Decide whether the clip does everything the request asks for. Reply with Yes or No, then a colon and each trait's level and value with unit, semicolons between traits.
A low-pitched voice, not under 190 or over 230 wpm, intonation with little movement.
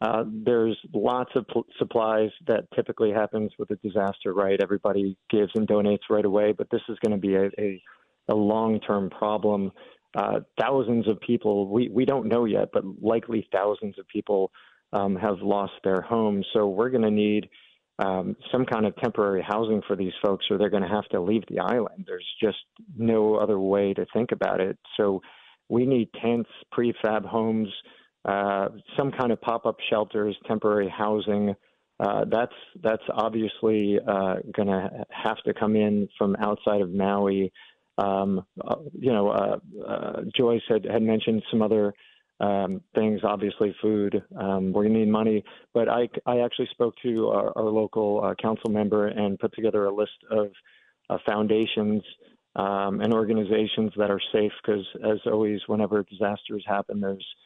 No: low, 105 Hz; average, 175 wpm; narrow, 1.7 semitones